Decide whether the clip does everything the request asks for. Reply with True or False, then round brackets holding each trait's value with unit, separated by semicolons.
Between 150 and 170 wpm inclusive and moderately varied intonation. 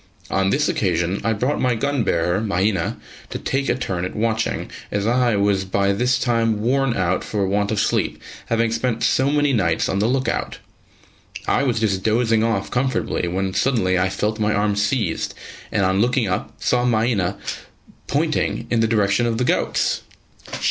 False (180 wpm; 3.8 semitones)